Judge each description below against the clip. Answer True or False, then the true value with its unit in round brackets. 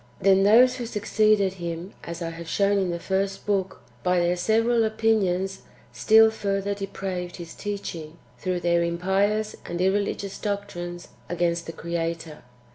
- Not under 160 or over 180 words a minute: False (145 wpm)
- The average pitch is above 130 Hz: True (190 Hz)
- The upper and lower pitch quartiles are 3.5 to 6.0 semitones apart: False (2.9 semitones)